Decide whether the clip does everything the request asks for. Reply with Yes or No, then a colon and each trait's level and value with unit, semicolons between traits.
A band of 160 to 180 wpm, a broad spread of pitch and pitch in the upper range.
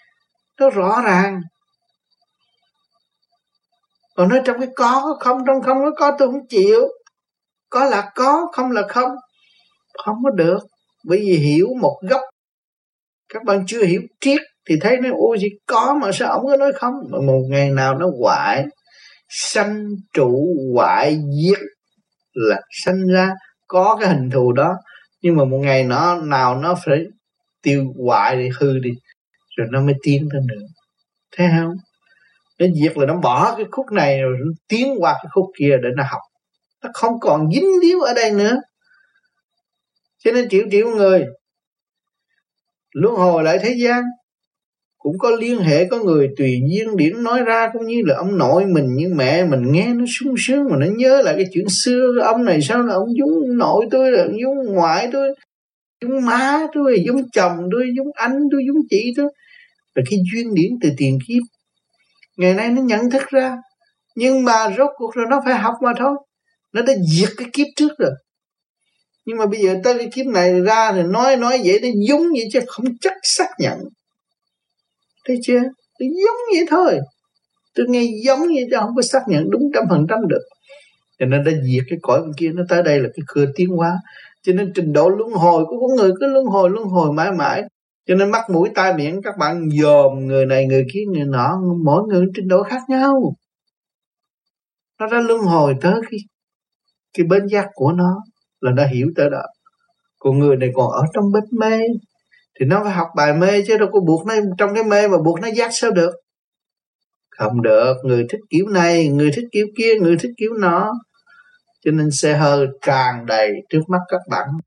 No: average, 195 wpm; wide, 6.9 semitones; high, 210 Hz